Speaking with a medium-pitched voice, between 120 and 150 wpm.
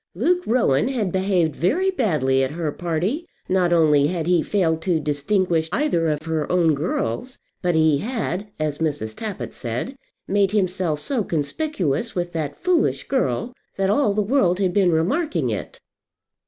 No: medium, 175 Hz; average, 160 wpm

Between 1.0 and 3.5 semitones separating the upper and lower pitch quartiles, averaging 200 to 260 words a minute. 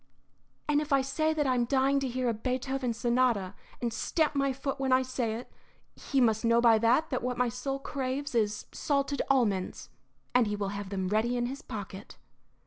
Yes: average, 3.2 semitones; fast, 205 wpm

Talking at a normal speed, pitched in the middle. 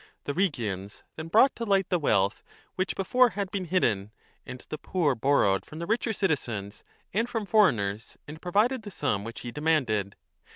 Yes: average, 180 wpm; medium, 155 Hz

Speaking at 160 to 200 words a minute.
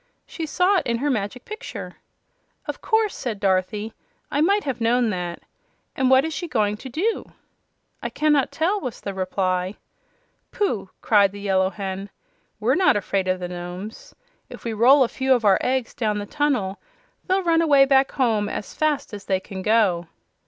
Yes: average, 180 wpm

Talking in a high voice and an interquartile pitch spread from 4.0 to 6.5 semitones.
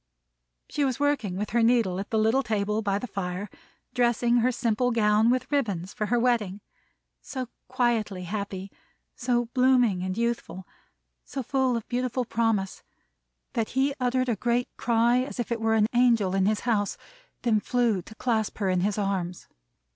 No: high, 230 Hz; average, 3.3 semitones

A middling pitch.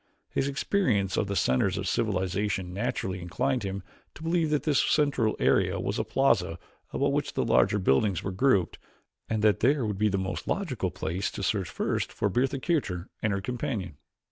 No: low, 105 Hz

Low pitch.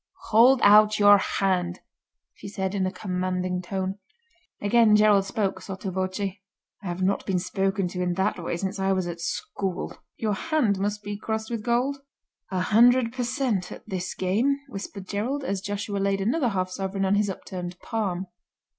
No: high, 195 Hz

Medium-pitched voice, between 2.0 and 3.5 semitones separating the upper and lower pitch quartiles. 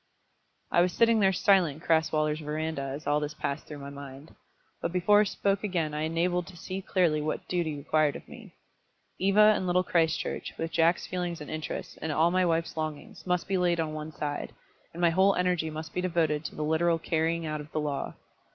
Yes: medium, 165 Hz; average, 2.8 semitones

